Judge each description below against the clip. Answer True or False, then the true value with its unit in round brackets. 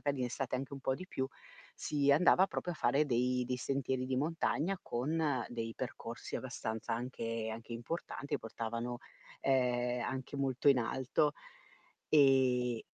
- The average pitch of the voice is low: True (130 Hz)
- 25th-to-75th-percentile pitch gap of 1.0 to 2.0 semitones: False (2.6 semitones)